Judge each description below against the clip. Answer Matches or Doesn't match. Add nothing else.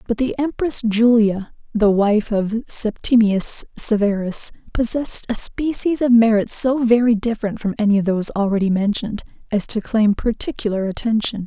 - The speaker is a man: Doesn't match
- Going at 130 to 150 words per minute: Matches